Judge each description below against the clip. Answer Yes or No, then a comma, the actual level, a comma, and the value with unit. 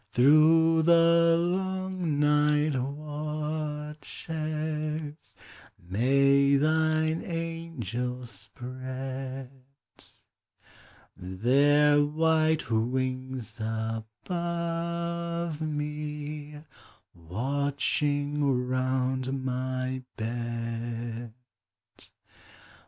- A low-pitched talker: No, medium, 145 Hz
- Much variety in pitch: No, average, 3.7 semitones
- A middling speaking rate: No, slow, 45 wpm